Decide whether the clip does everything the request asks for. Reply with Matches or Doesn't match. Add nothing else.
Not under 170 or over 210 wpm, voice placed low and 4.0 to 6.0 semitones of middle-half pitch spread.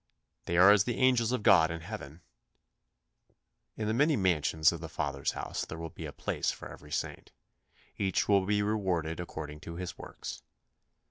Matches